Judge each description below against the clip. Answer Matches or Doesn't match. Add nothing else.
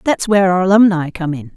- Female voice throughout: Matches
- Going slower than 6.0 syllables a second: Doesn't match